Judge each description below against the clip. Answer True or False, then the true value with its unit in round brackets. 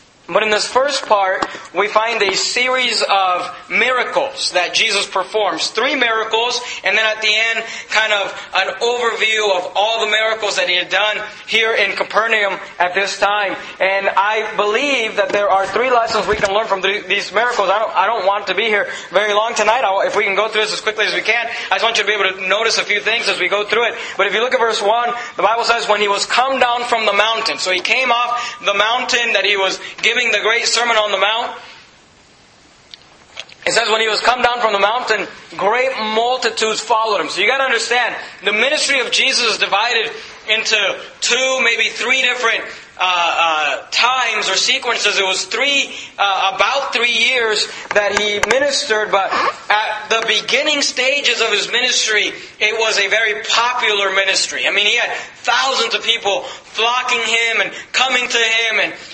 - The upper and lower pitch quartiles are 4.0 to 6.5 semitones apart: False (2.8 semitones)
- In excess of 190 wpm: True (200 wpm)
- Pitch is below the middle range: False (220 Hz)